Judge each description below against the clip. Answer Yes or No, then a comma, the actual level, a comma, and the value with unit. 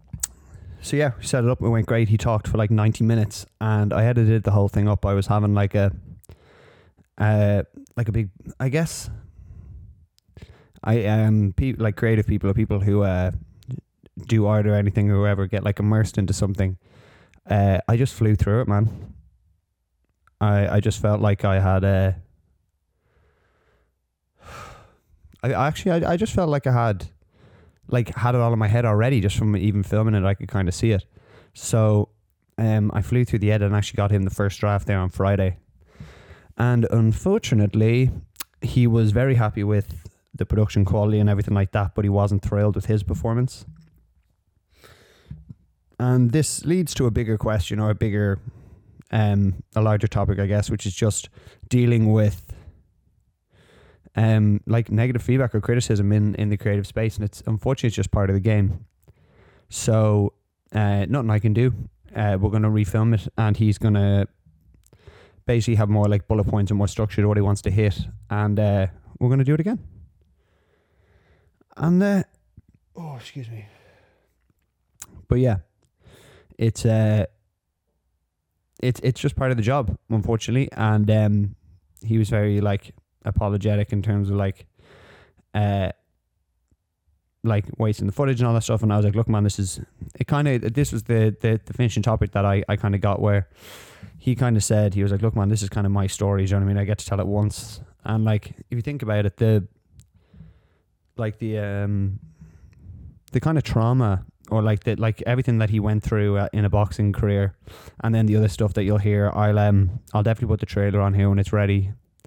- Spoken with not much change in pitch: Yes, narrow, 2.2 semitones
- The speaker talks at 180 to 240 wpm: Yes, average, 190 wpm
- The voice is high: No, low, 105 Hz